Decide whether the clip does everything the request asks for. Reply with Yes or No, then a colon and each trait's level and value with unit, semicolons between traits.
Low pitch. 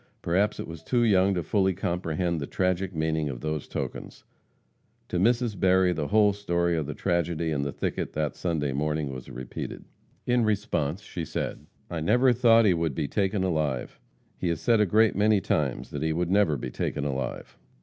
Yes: very low, 85 Hz